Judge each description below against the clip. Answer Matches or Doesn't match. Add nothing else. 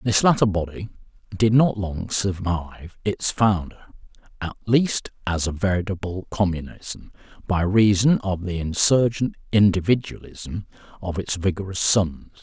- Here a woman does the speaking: Doesn't match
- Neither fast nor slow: Doesn't match